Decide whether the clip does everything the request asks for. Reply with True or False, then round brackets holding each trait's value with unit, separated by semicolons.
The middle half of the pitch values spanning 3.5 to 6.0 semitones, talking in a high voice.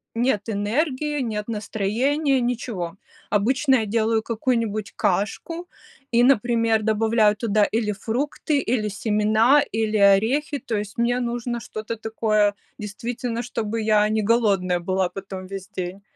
False (2.6 semitones; 220 Hz)